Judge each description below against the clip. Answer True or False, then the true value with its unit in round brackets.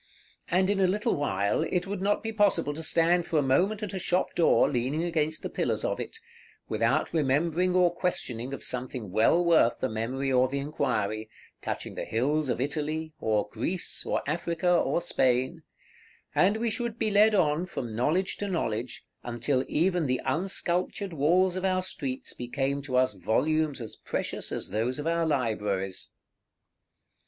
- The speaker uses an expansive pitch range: True (6.0 semitones)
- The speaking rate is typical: True (170 wpm)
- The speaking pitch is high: False (155 Hz)